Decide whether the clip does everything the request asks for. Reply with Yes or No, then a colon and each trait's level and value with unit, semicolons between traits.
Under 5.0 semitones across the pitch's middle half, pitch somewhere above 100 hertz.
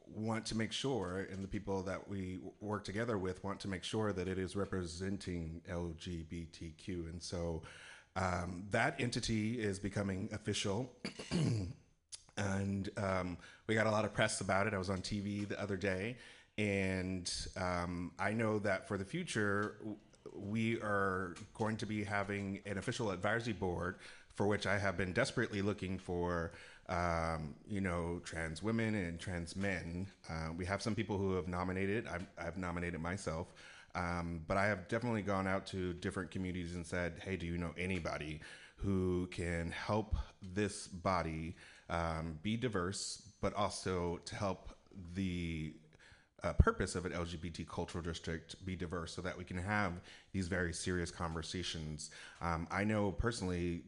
No: average, 2.9 semitones; very low, 95 Hz